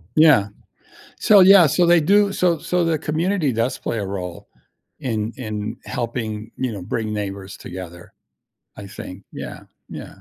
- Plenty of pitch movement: Yes, wide, 8.4 semitones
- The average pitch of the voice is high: No, low, 115 Hz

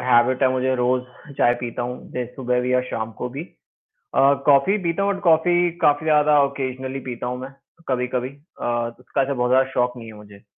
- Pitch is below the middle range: Yes, low, 130 Hz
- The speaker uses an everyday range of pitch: No, narrow, 2.1 semitones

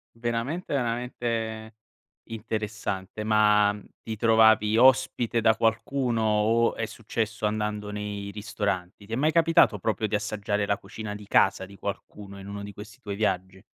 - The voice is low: Yes, low, 110 Hz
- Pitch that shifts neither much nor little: No, narrow, 1.8 semitones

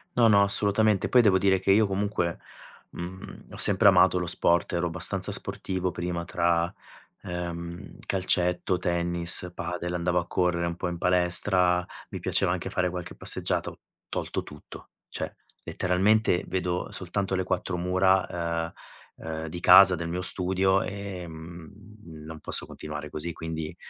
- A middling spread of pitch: No, narrow, 1.6 semitones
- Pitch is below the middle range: Yes, very low, 90 Hz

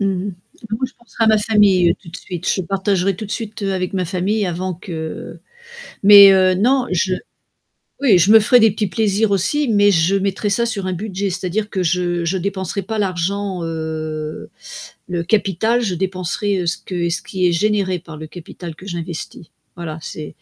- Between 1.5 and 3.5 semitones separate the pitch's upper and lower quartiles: Yes, average, 2.9 semitones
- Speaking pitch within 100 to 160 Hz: No, high, 190 Hz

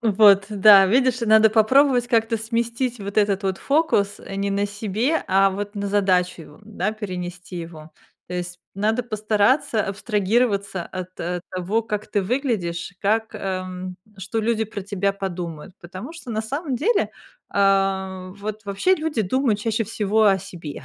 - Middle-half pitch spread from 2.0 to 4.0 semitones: Yes, average, 2.9 semitones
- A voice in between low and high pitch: No, high, 205 Hz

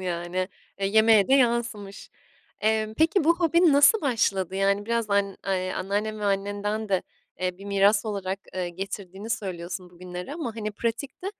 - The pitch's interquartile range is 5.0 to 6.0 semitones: No, average, 3.3 semitones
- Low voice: No, high, 205 Hz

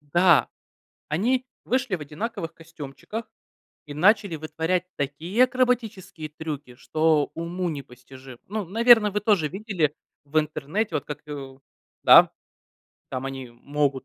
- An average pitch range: No, wide, 6.3 semitones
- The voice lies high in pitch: No, medium, 160 Hz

